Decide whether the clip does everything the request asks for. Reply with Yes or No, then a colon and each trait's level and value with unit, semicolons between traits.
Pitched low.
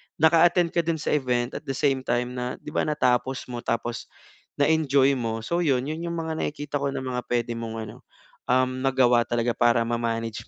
Yes: low, 130 Hz